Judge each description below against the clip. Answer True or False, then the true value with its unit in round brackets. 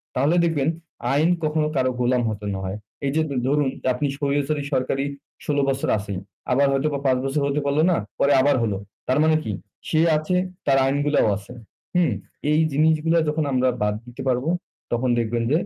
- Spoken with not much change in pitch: False (3.2 semitones)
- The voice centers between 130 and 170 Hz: True (140 Hz)